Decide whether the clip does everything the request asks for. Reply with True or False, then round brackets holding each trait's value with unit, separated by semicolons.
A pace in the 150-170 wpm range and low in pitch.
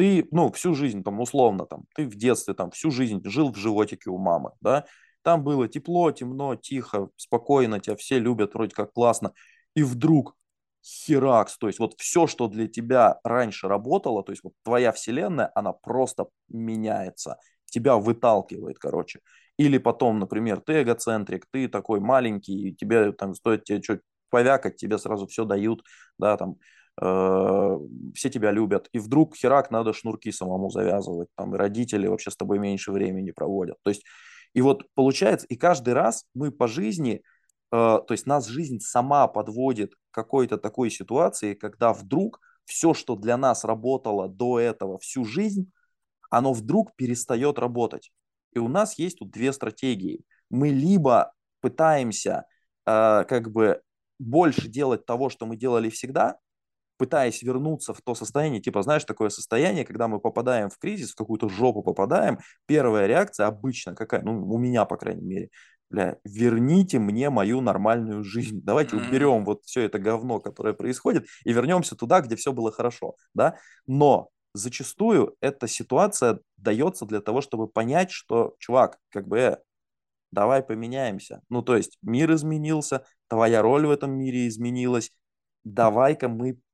True (160 wpm; 120 Hz)